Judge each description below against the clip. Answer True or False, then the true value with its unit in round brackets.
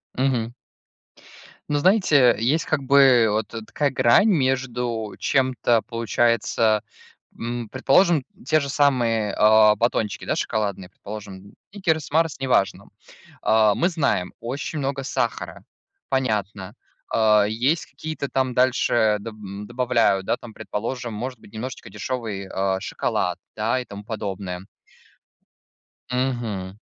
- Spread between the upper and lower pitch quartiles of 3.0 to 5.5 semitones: True (3.9 semitones)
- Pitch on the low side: True (120 Hz)